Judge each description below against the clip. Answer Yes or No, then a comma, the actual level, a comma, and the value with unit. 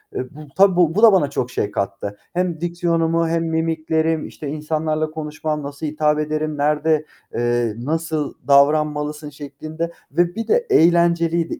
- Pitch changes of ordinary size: No, narrow, 2.1 semitones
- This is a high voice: No, medium, 155 Hz